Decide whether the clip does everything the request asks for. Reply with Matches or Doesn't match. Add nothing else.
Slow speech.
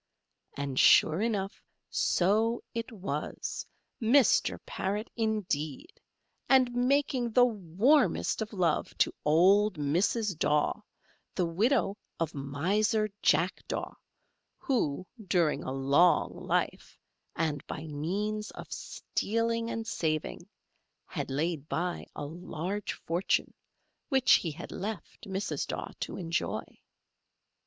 Matches